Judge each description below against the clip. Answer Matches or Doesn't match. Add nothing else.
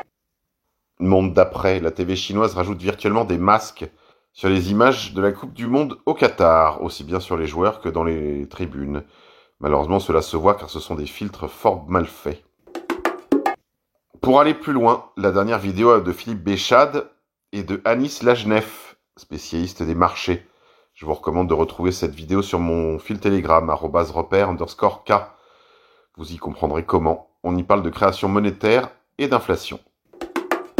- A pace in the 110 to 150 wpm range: Doesn't match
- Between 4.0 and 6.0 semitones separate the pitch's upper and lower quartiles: Matches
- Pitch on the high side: Doesn't match